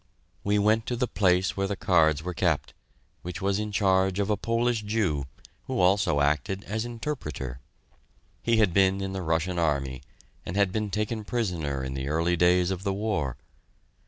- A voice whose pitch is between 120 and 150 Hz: No, very low, 95 Hz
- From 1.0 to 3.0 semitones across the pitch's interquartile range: No, average, 4.4 semitones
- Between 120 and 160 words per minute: No, average, 180 wpm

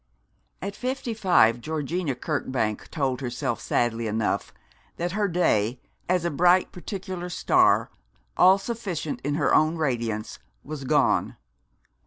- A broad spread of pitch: Yes, wide, 6.6 semitones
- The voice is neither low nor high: Yes, medium, 155 Hz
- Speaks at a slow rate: Yes, slow, 125 wpm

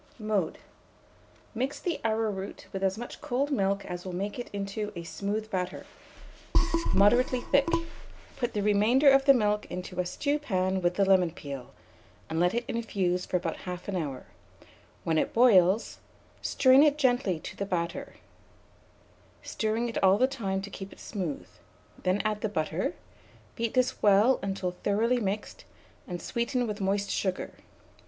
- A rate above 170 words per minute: No, average, 160 wpm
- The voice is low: No, high, 200 Hz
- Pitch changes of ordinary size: Yes, average, 4.3 semitones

